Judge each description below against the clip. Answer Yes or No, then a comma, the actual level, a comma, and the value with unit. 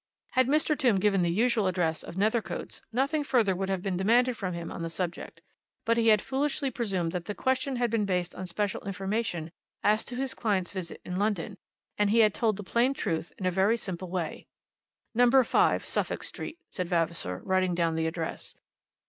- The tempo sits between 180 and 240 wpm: Yes, average, 200 wpm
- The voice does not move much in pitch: No, average, 4.7 semitones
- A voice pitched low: No, high, 200 Hz